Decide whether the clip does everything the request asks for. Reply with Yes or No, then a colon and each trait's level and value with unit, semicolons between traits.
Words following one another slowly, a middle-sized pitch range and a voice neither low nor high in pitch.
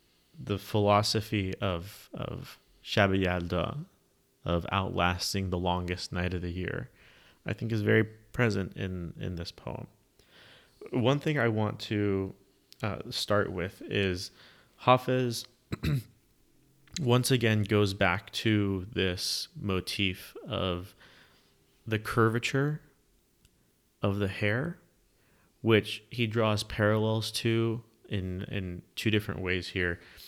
No: slow, 110 wpm; average, 3.7 semitones; low, 105 Hz